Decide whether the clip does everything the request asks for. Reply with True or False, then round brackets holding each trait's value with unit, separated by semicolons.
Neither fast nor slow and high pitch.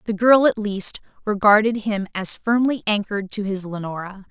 True (165 wpm; 205 Hz)